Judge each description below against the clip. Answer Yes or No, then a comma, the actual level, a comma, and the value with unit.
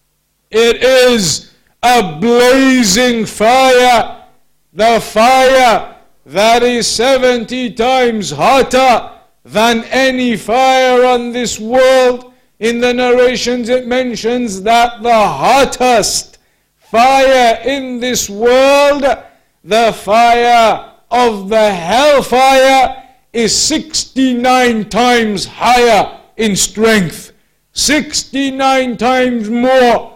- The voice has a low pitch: No, high, 245 Hz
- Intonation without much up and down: Yes, narrow, 2.2 semitones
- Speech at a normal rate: No, slow, 90 wpm